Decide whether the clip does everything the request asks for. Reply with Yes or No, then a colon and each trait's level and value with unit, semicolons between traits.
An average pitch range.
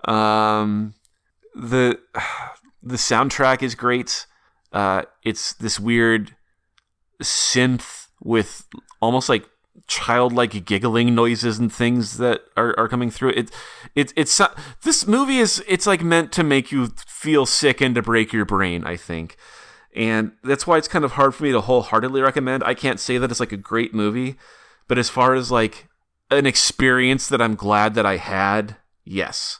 Yes: average, 3.4 semitones